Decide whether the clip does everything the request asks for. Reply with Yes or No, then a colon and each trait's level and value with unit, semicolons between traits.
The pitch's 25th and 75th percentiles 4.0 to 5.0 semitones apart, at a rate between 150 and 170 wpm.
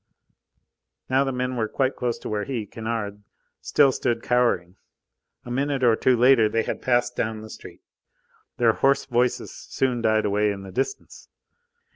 No: average, 2.9 semitones; average, 165 wpm